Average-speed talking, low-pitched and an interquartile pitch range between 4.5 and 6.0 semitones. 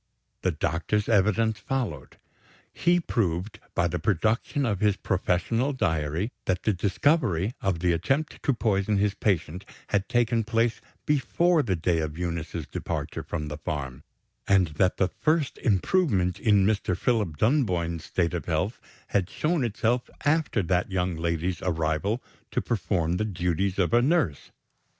Yes: average, 150 wpm; very low, 95 Hz; average, 5.2 semitones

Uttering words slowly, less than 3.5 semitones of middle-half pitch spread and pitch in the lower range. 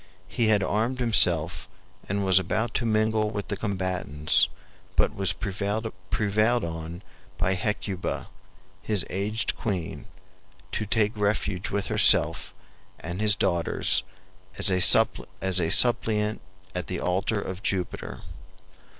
Yes: slow, 115 wpm; average, 2.8 semitones; low, 100 Hz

